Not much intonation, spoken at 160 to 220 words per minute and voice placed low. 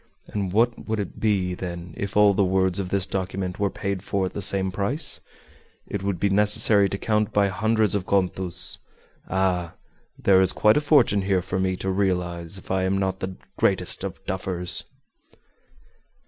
Yes: narrow, 1.6 semitones; average, 180 wpm; very low, 95 Hz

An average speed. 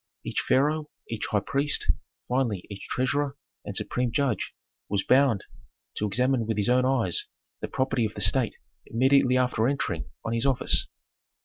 Yes: average, 155 wpm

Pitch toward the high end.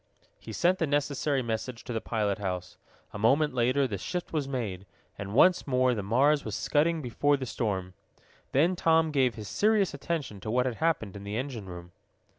No: low, 125 Hz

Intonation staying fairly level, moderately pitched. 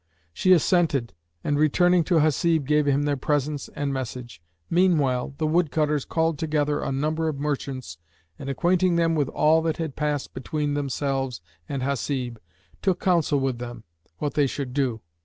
No: average, 3.0 semitones; medium, 145 Hz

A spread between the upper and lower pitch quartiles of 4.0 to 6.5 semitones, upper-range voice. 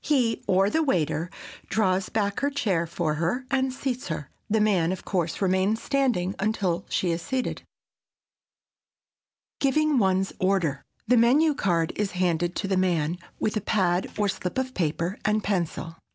Yes: average, 4.9 semitones; high, 195 Hz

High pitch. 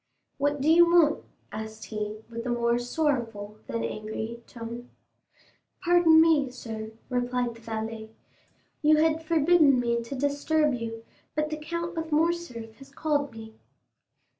Yes: very high, 250 Hz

